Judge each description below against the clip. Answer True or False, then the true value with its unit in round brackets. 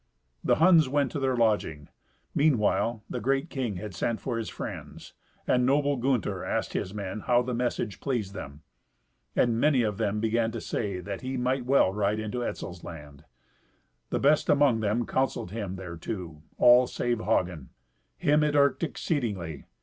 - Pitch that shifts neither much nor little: True (5.0 semitones)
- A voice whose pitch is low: True (115 Hz)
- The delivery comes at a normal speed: True (165 wpm)